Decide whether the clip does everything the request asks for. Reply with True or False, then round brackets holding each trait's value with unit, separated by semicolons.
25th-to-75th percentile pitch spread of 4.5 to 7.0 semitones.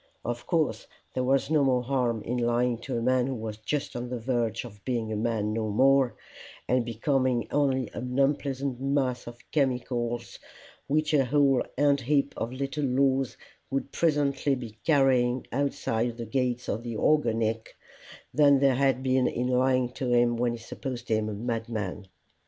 False (2.6 semitones)